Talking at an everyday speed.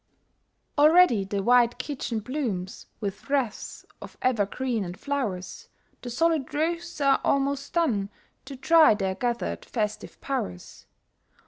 No: slow, 120 wpm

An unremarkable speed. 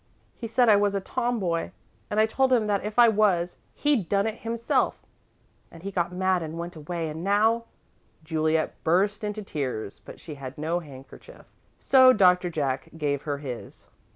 Yes: average, 180 wpm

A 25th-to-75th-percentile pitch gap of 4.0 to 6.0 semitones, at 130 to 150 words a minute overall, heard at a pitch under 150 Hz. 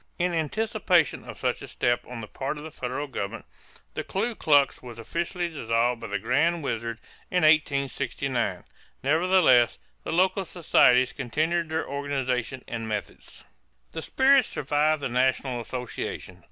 Yes: wide, 5.4 semitones; average, 145 wpm; medium, 140 Hz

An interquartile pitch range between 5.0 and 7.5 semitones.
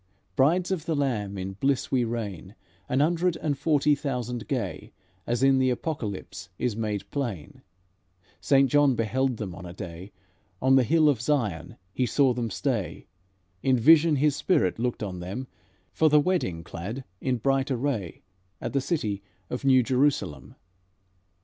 Yes: average, 5.3 semitones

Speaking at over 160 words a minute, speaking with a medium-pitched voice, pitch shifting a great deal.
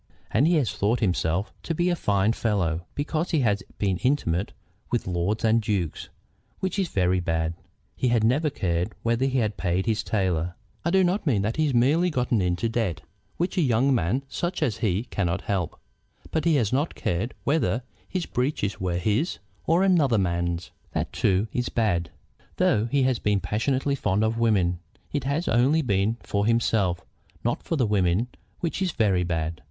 No: average, 185 wpm; low, 110 Hz; wide, 6.9 semitones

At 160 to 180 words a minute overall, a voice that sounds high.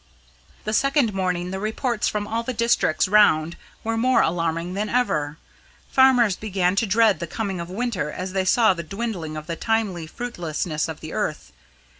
Yes: average, 175 wpm; high, 195 Hz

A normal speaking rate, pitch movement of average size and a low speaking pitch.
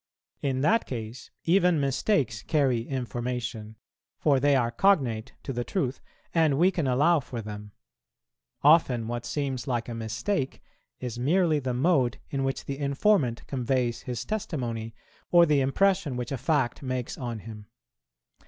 Yes: average, 150 wpm; average, 4.1 semitones; low, 130 Hz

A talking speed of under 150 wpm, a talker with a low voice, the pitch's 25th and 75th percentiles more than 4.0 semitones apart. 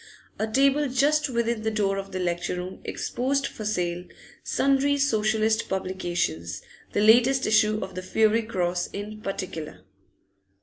No: average, 140 wpm; high, 215 Hz; average, 4.9 semitones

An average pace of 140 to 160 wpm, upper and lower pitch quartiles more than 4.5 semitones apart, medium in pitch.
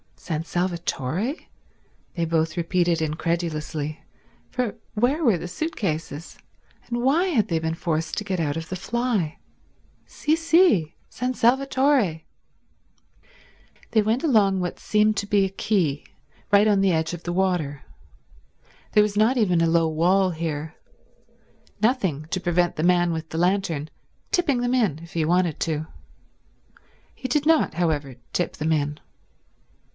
Yes: average, 145 wpm; average, 5.2 semitones; medium, 180 Hz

